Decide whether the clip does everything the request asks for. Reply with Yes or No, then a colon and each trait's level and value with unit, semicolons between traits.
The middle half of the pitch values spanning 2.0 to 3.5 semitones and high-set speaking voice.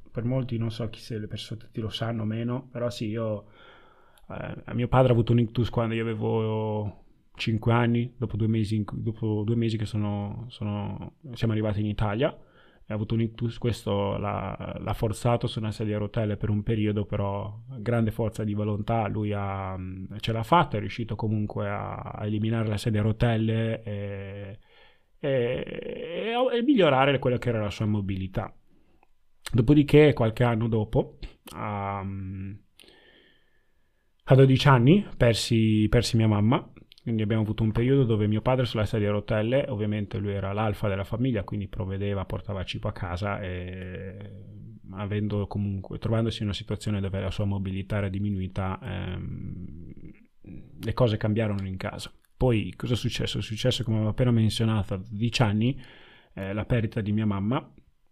No: narrow, 2.5 semitones; low, 110 Hz